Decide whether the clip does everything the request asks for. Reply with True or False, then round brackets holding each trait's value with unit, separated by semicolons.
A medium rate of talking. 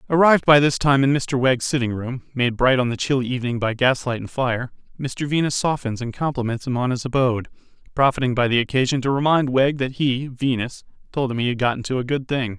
False (225 wpm)